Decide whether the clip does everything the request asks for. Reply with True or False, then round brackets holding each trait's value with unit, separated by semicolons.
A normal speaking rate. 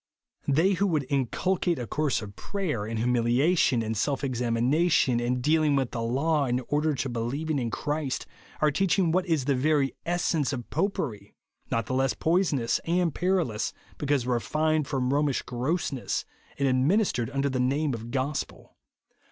True (170 wpm)